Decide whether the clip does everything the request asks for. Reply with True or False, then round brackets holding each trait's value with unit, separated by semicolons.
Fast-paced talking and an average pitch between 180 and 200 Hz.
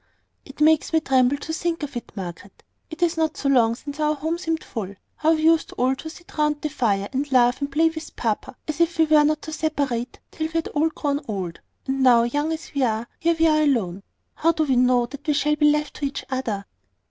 False (240 wpm; 290 Hz)